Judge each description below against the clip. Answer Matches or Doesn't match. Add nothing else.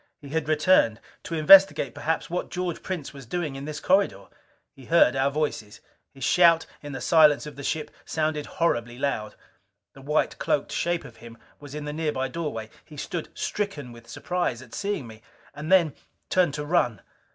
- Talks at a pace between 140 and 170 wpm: Doesn't match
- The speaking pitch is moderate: Matches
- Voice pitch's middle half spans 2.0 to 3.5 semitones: Doesn't match